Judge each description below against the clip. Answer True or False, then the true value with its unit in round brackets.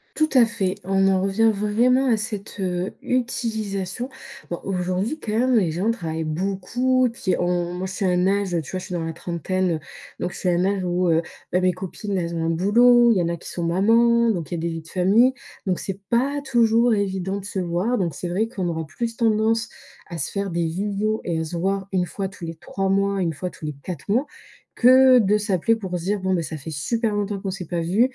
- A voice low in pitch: False (195 Hz)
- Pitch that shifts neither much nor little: True (4.2 semitones)